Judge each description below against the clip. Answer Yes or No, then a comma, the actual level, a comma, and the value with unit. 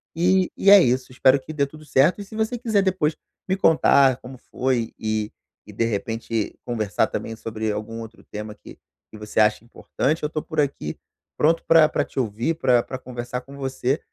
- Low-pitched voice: Yes, low, 130 Hz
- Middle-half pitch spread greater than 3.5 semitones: Yes, wide, 5.6 semitones